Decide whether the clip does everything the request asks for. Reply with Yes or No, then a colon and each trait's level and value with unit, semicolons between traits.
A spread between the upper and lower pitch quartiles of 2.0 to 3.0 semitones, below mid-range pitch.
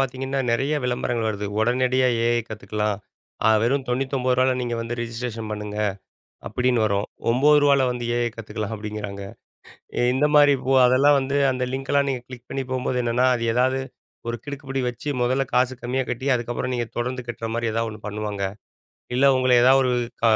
Yes: narrow, 2.4 semitones; low, 125 Hz